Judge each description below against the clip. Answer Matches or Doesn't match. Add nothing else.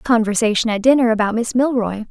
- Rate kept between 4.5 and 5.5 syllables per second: Doesn't match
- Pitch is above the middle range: Matches